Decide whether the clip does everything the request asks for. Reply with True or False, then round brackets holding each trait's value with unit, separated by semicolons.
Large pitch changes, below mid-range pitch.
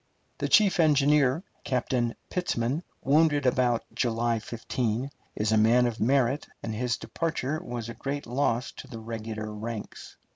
False (3.6 semitones; 125 Hz)